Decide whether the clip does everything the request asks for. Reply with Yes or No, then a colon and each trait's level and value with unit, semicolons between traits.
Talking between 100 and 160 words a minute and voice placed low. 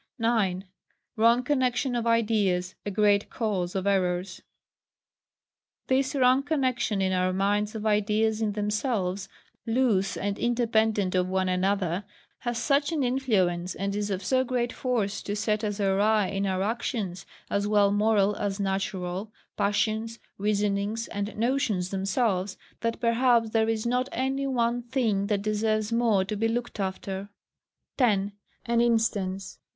No: average, 145 wpm; high, 210 Hz